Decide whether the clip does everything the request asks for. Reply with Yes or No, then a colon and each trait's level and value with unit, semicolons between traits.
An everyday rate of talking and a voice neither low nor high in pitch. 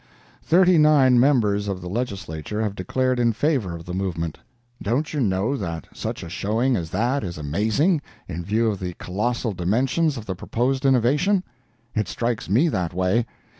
No: average, 170 wpm; low, 110 Hz